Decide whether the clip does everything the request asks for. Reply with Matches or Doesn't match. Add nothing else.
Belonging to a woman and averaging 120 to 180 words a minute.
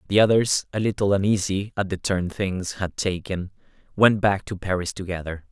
Doesn't match